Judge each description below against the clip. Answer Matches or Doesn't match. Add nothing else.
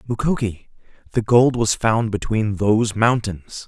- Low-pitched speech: Matches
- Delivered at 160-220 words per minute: Doesn't match